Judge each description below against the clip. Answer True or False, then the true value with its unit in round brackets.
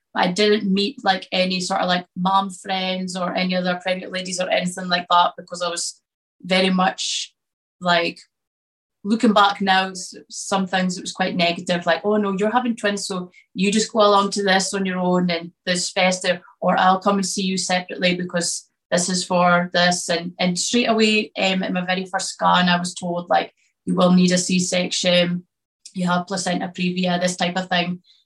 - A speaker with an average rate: True (195 wpm)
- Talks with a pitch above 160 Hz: True (185 Hz)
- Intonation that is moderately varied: False (1.4 semitones)